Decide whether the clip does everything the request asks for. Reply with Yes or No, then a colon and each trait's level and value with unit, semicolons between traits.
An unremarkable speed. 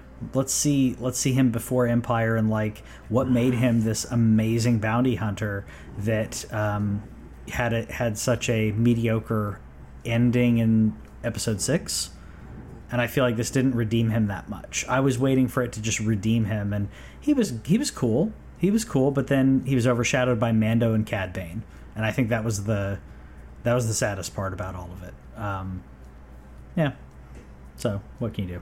Yes: average, 180 wpm